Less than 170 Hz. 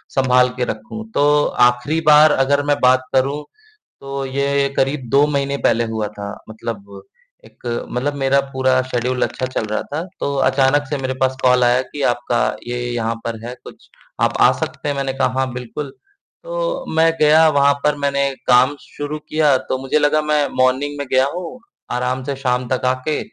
Yes: low, 135 Hz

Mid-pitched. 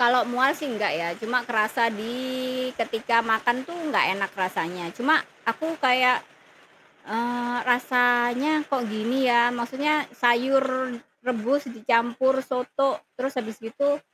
No: high, 245 Hz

